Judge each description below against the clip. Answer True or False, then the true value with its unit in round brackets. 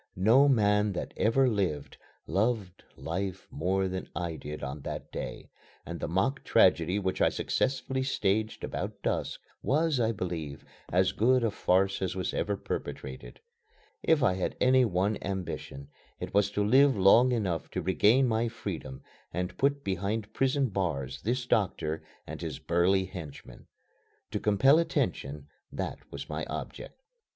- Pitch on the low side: True (100 Hz)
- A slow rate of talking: False (150 wpm)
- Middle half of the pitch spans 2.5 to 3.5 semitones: False (4.8 semitones)